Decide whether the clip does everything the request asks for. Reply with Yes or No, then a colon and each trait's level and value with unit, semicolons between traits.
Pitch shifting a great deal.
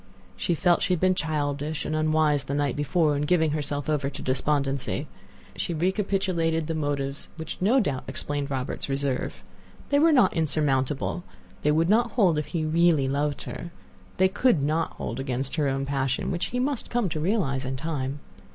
No: average, 3.8 semitones